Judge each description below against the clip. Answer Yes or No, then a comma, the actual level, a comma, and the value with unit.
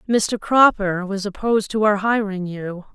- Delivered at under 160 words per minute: No, average, 165 wpm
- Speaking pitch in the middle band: No, high, 205 Hz